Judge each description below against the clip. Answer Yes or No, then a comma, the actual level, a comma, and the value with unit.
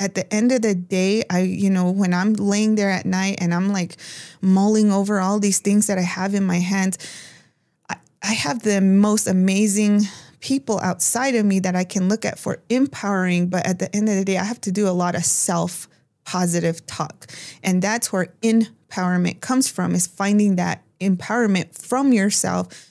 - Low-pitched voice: No, high, 190 Hz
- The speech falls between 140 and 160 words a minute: No, average, 195 wpm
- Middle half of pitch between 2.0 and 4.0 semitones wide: Yes, narrow, 2.5 semitones